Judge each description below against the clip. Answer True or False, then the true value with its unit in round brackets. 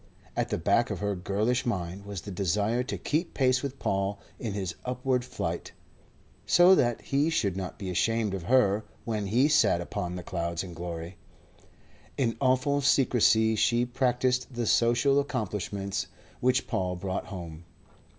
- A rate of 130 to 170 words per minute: True (160 wpm)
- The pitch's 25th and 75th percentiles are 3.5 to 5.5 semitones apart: True (5.0 semitones)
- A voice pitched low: True (110 Hz)